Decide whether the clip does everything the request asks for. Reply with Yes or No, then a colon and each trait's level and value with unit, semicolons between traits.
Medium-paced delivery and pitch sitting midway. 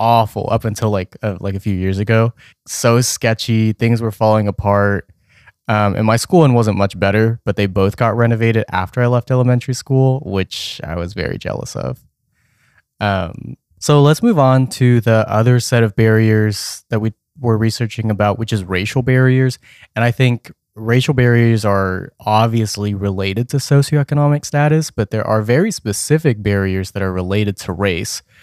No: average, 170 wpm; low, 110 Hz